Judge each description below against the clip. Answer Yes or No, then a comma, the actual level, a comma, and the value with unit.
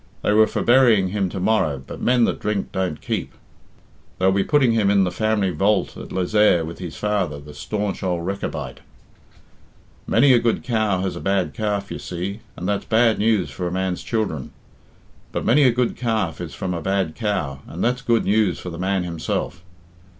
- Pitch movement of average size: Yes, average, 3.5 semitones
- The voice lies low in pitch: Yes, low, 100 Hz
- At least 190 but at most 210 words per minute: Yes, average, 195 wpm